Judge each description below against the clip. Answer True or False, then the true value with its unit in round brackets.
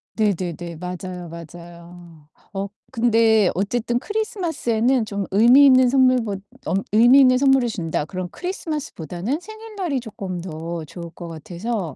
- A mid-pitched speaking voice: False (210 Hz)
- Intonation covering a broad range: True (6.7 semitones)